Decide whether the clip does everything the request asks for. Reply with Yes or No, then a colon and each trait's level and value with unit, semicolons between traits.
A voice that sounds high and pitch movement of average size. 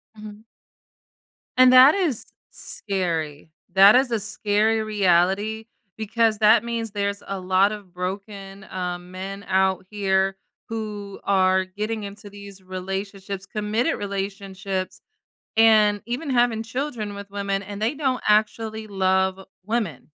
No: high, 205 Hz; narrow, 2.3 semitones